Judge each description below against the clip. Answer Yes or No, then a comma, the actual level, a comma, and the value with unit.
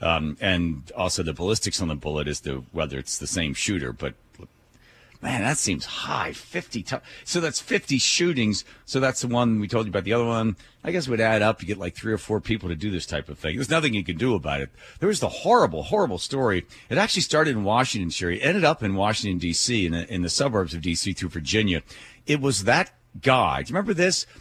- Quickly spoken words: Yes, fast, 235 wpm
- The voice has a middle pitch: No, low, 105 Hz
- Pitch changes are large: Yes, wide, 6.6 semitones